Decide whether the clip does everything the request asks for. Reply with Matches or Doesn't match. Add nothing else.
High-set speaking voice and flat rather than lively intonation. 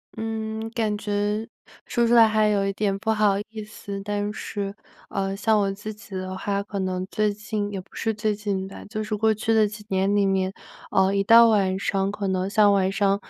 Matches